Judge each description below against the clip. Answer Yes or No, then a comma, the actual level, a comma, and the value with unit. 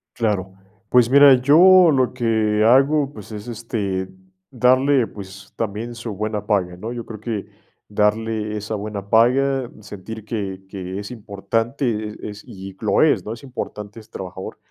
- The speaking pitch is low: Yes, low, 110 Hz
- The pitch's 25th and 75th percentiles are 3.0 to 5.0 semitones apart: Yes, average, 3.3 semitones